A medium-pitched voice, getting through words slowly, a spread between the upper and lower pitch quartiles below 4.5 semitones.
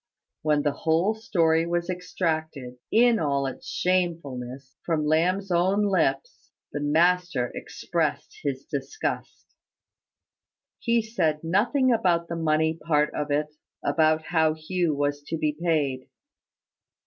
Yes: medium, 160 Hz; slow, 125 wpm; average, 3.4 semitones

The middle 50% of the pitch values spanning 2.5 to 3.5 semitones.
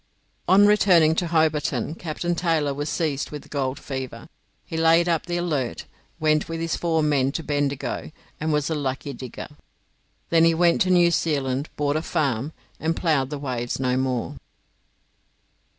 Yes: average, 3.1 semitones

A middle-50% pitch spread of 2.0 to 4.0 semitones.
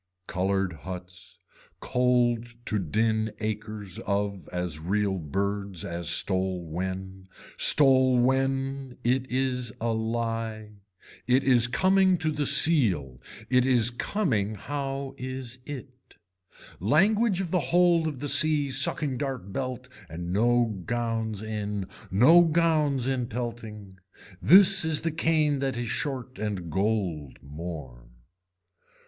No: wide, 5.5 semitones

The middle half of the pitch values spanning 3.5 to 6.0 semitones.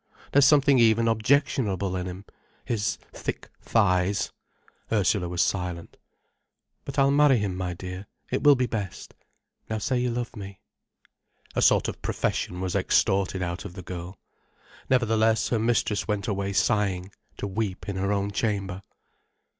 Yes: average, 3.8 semitones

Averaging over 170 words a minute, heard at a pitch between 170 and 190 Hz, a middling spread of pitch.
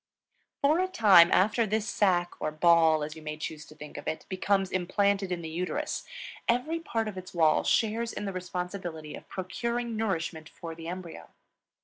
Yes: average, 180 wpm; medium, 185 Hz; average, 4.7 semitones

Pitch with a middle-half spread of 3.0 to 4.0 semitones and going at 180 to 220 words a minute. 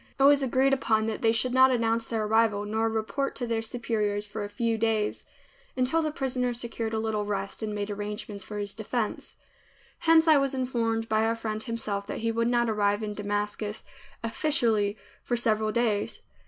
No: narrow, 2.5 semitones; average, 190 wpm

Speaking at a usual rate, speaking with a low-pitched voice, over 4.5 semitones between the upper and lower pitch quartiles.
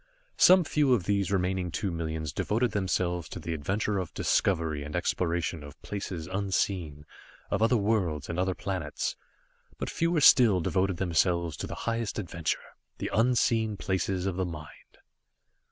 No: average, 155 wpm; very low, 95 Hz; average, 3.8 semitones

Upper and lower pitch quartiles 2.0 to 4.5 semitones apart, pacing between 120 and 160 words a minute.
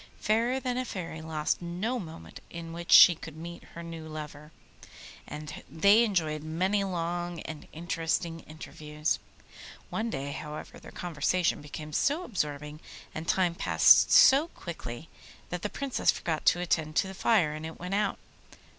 Yes: average, 3.7 semitones; average, 155 wpm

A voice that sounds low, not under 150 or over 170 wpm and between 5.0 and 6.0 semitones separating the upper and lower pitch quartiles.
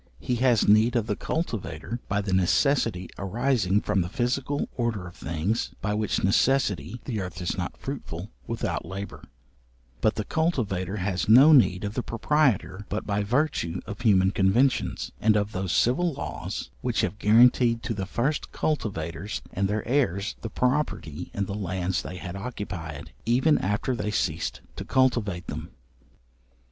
No: low, 105 Hz; average, 160 wpm; average, 4.6 semitones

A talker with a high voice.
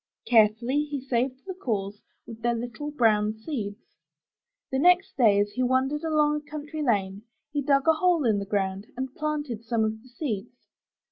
Yes: very high, 250 Hz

